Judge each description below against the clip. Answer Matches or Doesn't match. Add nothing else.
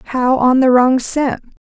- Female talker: Matches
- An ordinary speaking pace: Matches